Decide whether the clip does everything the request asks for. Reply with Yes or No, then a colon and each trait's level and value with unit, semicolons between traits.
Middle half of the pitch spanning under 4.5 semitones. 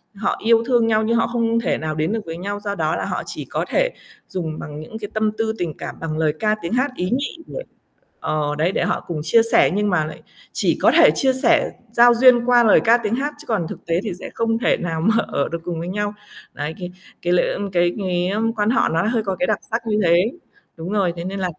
No: average, 5.2 semitones